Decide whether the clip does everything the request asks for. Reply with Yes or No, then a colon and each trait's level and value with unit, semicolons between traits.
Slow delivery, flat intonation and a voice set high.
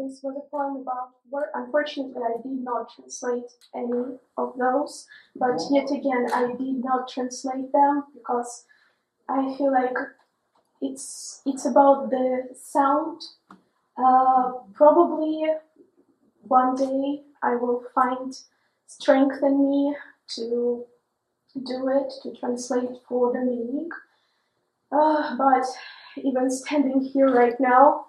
Yes: slow, 120 wpm; narrow, 2.0 semitones; very high, 265 Hz